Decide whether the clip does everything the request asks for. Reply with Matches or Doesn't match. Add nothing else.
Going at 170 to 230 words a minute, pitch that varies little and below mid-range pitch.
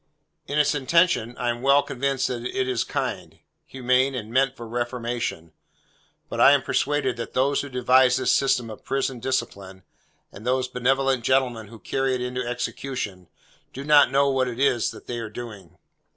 Matches